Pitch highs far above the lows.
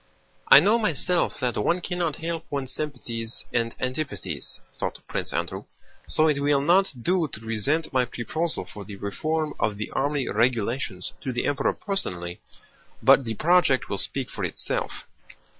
Yes: wide, 5.9 semitones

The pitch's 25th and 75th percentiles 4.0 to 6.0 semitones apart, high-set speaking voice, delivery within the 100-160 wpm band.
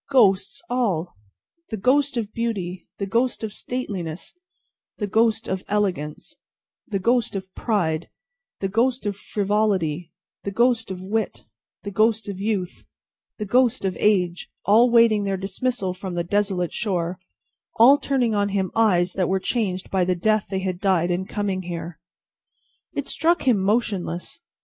No: average, 3.6 semitones; high, 200 Hz; average, 155 wpm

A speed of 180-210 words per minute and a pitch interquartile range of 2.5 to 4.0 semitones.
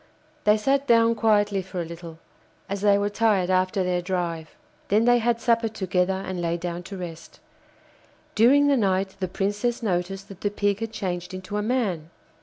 Yes: average, 185 wpm; average, 3.4 semitones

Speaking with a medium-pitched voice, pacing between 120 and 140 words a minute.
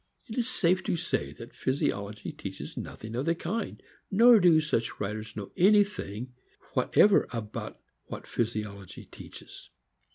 No: low, 130 Hz; slow, 135 wpm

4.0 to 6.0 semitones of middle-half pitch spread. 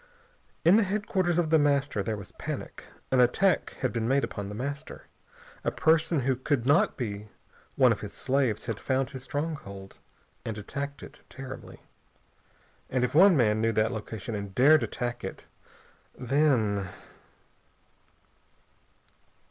Yes: average, 5.1 semitones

